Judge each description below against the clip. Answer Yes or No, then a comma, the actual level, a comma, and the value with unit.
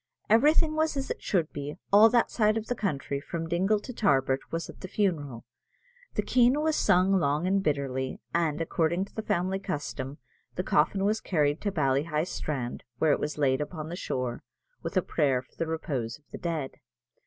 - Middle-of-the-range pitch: Yes, medium, 165 Hz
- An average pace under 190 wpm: No, average, 195 wpm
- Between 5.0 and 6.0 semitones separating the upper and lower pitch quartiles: Yes, wide, 5.6 semitones